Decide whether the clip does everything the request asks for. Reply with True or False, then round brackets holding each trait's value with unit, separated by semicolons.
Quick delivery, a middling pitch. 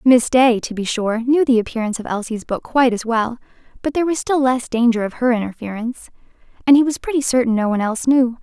False (230 wpm; 245 Hz)